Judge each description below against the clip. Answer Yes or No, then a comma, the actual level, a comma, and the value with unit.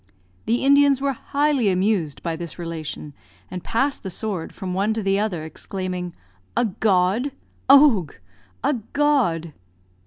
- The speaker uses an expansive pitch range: Yes, wide, 7.2 semitones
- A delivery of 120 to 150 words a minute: Yes, slow, 135 wpm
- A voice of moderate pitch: No, high, 200 Hz